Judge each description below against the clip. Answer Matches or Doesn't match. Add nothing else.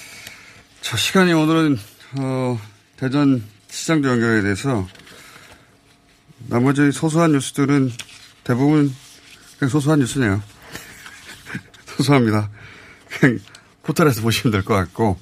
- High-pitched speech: Doesn't match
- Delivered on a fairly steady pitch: Doesn't match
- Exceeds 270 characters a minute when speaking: Doesn't match